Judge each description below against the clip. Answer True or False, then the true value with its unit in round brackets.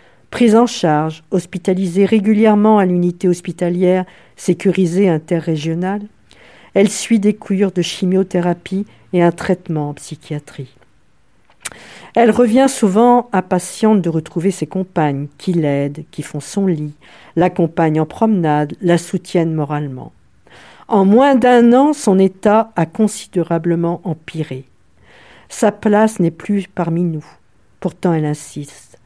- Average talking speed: False (120 wpm)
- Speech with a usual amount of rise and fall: True (4.1 semitones)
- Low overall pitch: False (180 Hz)